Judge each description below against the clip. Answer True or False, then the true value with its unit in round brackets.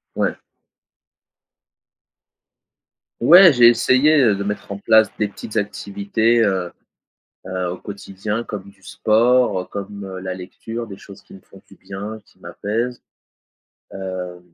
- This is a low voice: True (105 Hz)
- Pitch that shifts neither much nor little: True (3.2 semitones)